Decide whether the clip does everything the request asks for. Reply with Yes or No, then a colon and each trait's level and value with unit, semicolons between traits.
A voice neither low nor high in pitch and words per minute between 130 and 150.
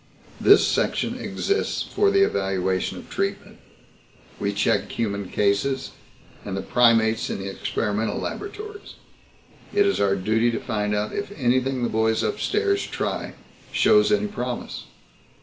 No: low, 115 Hz; average, 140 wpm